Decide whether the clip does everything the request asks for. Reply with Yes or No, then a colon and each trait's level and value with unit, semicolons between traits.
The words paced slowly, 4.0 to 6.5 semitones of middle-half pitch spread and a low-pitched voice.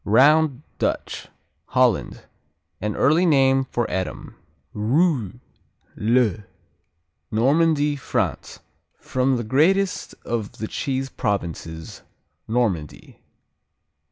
Yes: slow, 85 wpm; average, 5.2 semitones; low, 130 Hz